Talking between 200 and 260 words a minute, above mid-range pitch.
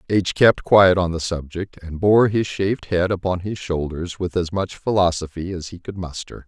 No: fast, 205 wpm; very low, 90 Hz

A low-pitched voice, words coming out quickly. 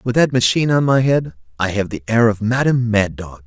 Yes: low, 115 Hz; fast, 240 wpm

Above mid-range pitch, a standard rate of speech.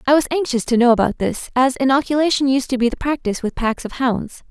No: very high, 255 Hz; fast, 240 wpm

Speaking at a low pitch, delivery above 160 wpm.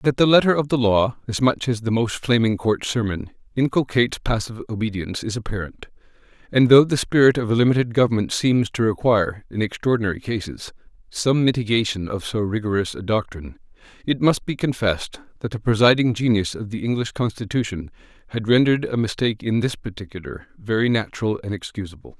Yes: low, 115 Hz; average, 170 wpm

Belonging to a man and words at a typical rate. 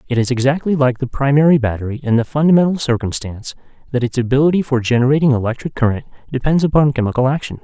Yes: male; average, 175 wpm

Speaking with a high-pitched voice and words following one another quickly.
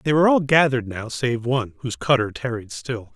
No: low, 125 Hz; fast, 210 wpm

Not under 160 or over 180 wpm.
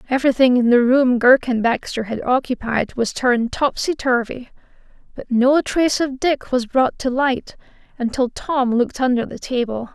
Yes: average, 170 wpm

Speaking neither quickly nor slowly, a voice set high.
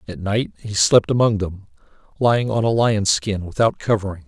No: average, 180 wpm; low, 105 Hz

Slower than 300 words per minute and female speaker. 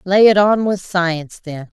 Yes: average, 200 wpm; female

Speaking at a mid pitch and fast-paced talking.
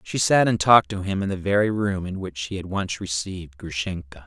No: very low, 95 Hz; fast, 240 wpm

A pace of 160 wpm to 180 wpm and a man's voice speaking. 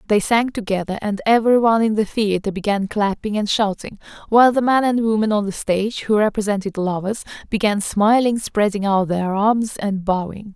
No: average, 170 wpm; female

